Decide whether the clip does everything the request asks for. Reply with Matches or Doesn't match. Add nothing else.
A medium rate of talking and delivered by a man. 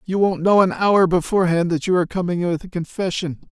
Doesn't match